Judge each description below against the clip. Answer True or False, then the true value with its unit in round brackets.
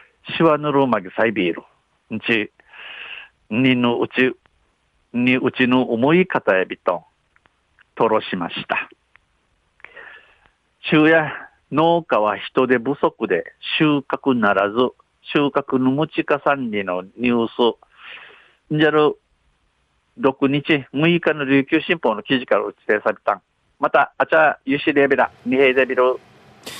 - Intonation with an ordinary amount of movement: True (4.2 semitones)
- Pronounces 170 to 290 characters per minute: True (225 characters per minute)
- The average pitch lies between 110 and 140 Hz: True (135 Hz)